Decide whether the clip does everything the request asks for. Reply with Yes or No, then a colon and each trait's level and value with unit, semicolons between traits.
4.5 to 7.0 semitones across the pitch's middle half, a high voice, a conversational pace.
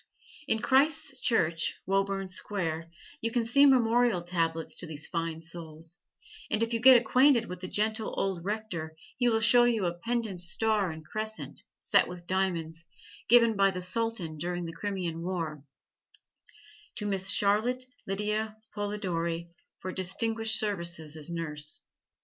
Yes: average, 4.8 semitones; high, 195 Hz; average, 145 wpm